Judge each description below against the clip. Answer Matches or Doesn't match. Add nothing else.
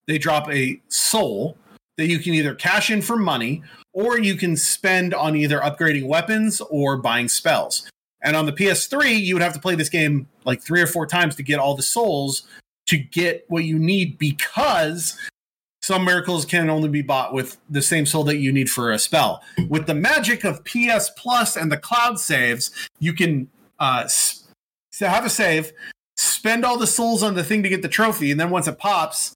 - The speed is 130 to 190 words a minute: Doesn't match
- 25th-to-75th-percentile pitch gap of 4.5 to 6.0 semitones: Matches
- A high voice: Doesn't match